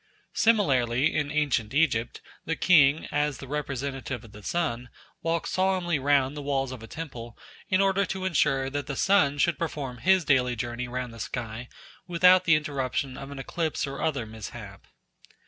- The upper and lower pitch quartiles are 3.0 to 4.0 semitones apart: No, average, 4.6 semitones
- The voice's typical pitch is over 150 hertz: No, medium, 140 Hz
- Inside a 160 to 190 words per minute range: Yes, average, 170 wpm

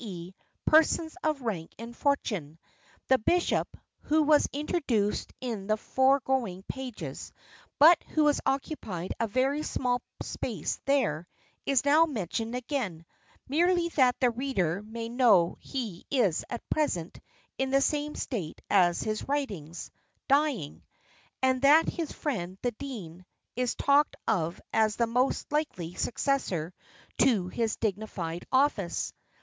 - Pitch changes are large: Yes, wide, 6.7 semitones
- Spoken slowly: Yes, slow, 130 wpm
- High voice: Yes, high, 245 Hz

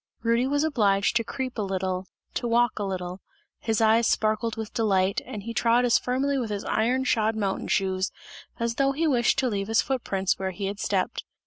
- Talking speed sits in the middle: No, fast, 210 wpm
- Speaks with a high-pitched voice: Yes, high, 225 Hz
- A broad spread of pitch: No, average, 3.7 semitones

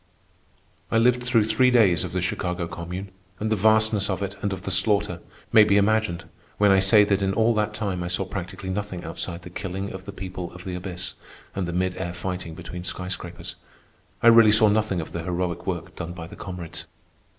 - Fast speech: Yes, fast, 215 wpm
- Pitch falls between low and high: No, very low, 95 Hz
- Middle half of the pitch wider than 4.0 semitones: No, average, 2.9 semitones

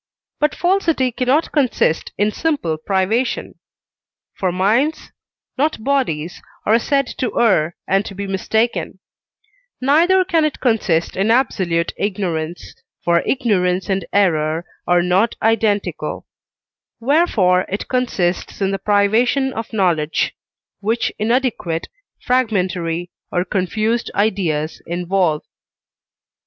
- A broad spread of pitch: Yes, wide, 5.9 semitones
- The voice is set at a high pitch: Yes, high, 205 Hz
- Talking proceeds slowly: Yes, slow, 110 wpm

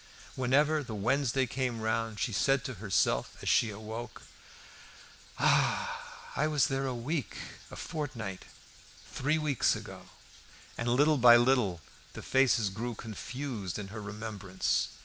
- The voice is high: No, low, 120 Hz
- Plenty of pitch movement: No, average, 4.0 semitones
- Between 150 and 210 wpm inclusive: No, slow, 135 wpm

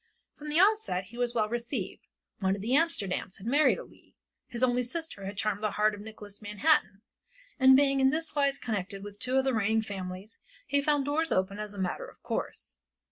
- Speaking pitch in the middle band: No, high, 225 Hz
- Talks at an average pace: No, fast, 215 wpm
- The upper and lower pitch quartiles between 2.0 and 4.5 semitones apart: No, wide, 5.5 semitones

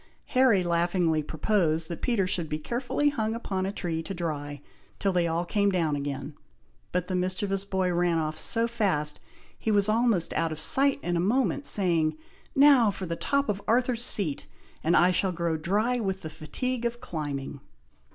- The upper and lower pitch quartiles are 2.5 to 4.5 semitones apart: No, average, 5.3 semitones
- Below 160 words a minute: No, average, 180 wpm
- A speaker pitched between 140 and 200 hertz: Yes, medium, 185 Hz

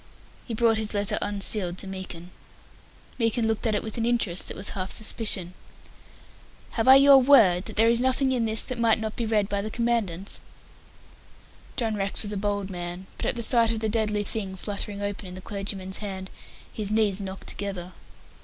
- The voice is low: No, high, 210 Hz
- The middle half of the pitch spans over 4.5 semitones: No, average, 2.8 semitones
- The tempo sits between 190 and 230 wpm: Yes, average, 195 wpm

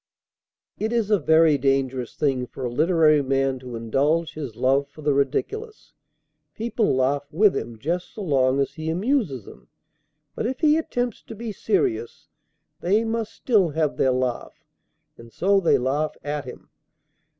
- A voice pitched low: No, medium, 155 Hz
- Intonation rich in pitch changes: Yes, wide, 8.1 semitones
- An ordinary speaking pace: Yes, average, 160 wpm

